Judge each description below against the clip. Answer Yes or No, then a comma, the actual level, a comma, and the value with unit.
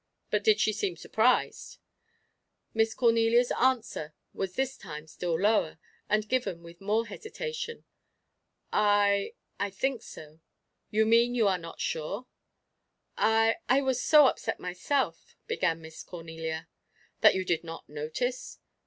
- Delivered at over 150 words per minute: No, slow, 135 wpm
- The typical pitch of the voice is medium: No, high, 210 Hz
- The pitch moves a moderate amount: No, wide, 6.2 semitones